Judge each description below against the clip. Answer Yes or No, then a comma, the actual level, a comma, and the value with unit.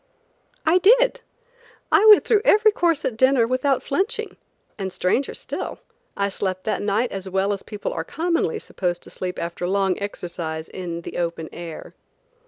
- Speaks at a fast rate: No, average, 165 wpm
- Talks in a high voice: Yes, high, 200 Hz